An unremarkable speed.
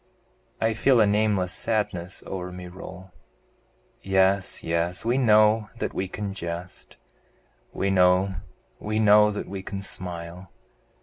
No: slow, 130 wpm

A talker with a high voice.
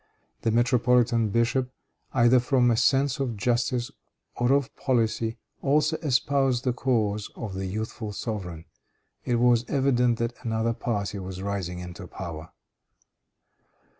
No: low, 120 Hz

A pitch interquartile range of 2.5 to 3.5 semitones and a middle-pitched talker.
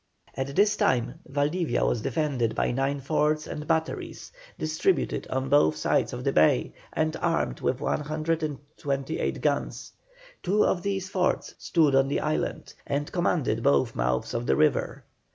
Yes: average, 3.2 semitones; medium, 150 Hz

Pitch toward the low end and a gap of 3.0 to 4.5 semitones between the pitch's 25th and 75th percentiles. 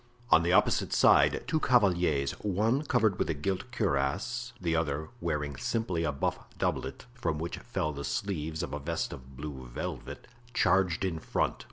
No: very low, 85 Hz; wide, 5.4 semitones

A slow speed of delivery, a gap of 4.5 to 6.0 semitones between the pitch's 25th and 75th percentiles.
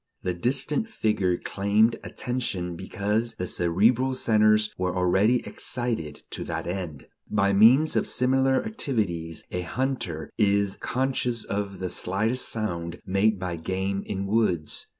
Yes: slow, 130 wpm; average, 4.8 semitones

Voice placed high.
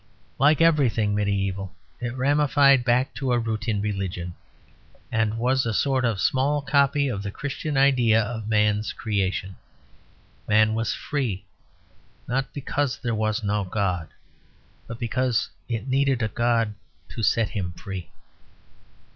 No: low, 115 Hz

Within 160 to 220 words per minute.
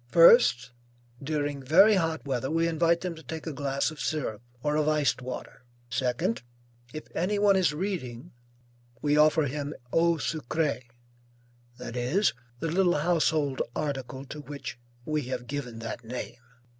No: average, 150 wpm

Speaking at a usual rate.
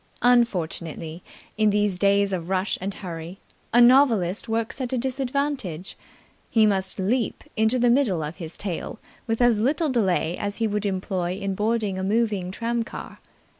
Yes: average, 160 wpm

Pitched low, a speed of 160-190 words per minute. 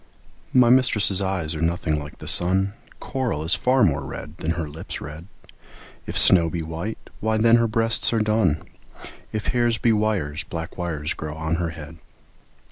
Yes: very low, 85 Hz; average, 175 wpm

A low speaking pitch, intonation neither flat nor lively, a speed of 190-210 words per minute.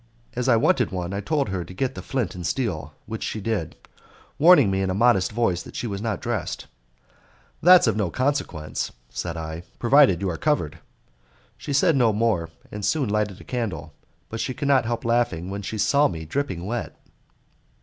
No: low, 110 Hz; wide, 5.7 semitones; average, 195 wpm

